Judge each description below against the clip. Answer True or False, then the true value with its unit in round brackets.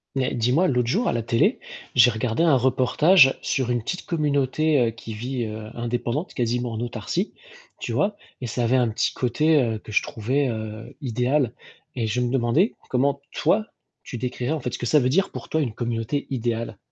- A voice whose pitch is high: False (125 Hz)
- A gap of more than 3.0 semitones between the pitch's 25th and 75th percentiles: True (3.5 semitones)